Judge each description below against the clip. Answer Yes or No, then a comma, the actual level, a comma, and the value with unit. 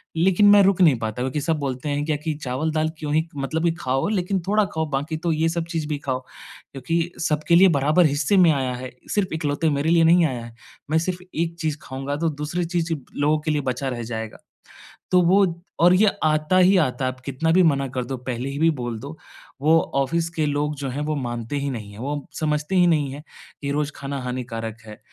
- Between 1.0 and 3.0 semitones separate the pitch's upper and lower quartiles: No, average, 3.7 semitones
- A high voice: No, medium, 150 Hz